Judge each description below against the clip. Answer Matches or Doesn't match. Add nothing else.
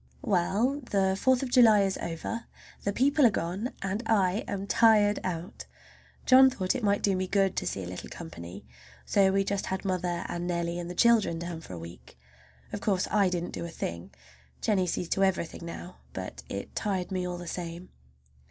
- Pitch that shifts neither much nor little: Matches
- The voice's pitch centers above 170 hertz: Matches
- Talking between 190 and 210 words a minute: Matches